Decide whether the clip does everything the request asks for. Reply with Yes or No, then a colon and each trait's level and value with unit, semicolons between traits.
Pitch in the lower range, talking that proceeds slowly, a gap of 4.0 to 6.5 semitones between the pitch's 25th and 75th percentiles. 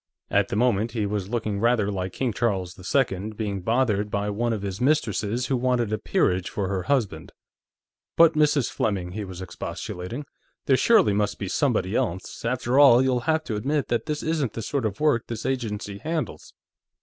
No: low, 115 Hz; average, 185 wpm; average, 4.5 semitones